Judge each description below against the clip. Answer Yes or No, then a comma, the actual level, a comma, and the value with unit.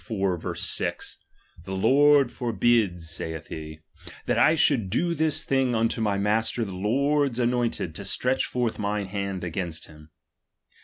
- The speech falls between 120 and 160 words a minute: Yes, average, 140 wpm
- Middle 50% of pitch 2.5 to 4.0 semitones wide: No, average, 5.3 semitones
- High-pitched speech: No, low, 110 Hz